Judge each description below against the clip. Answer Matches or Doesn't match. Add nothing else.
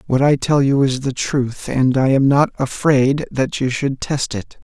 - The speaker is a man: Matches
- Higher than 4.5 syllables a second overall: Doesn't match